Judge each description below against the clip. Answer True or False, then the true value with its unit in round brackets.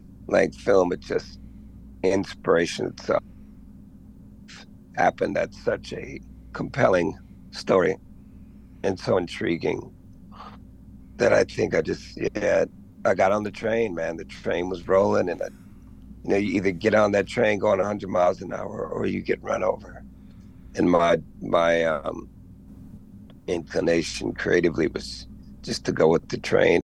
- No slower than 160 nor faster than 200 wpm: False (145 wpm)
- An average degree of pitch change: True (3.6 semitones)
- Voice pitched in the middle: False (95 Hz)